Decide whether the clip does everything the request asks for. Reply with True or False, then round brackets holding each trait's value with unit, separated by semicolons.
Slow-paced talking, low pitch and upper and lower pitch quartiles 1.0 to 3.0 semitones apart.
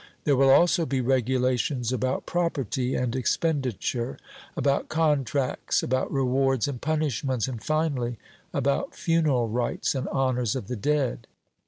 True (130 wpm; 130 Hz; 2.7 semitones)